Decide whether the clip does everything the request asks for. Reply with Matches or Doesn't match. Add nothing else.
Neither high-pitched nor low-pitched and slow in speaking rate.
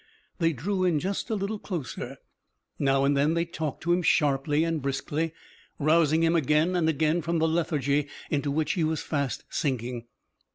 Doesn't match